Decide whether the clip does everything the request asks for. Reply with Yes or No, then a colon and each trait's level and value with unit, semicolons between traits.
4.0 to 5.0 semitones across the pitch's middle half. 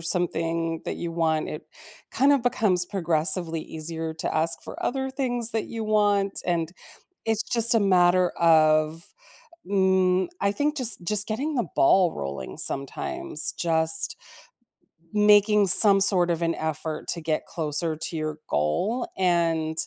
Yes: average, 4.6 semitones